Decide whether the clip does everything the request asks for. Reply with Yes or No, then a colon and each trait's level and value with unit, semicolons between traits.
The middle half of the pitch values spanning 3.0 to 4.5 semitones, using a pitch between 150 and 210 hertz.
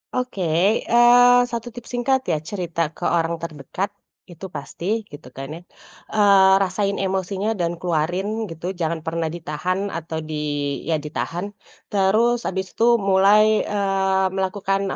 Yes: average, 3.6 semitones; high, 190 Hz